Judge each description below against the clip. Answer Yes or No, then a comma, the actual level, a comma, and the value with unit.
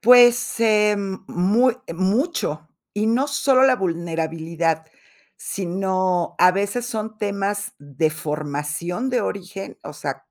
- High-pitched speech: Yes, high, 195 Hz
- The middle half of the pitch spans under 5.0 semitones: No, average, 5.3 semitones